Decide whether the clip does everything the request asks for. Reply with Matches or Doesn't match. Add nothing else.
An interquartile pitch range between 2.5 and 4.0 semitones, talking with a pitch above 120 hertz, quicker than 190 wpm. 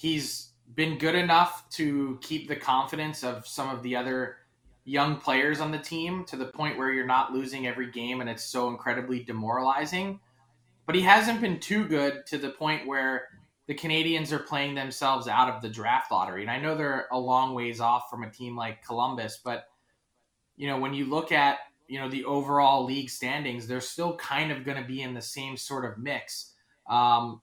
Matches